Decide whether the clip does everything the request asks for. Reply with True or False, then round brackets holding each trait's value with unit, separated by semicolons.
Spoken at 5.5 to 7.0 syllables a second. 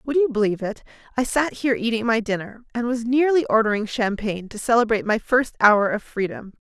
True (5.9 syllables/s)